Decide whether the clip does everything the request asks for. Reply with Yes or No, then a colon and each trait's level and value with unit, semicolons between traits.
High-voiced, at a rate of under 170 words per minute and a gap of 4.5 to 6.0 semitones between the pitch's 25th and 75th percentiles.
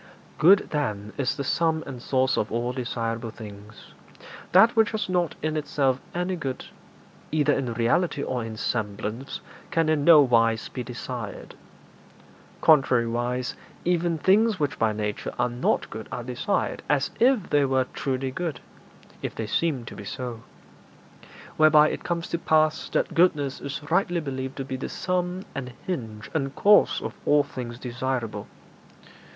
No: low, 135 Hz; average, 155 wpm; average, 5.2 semitones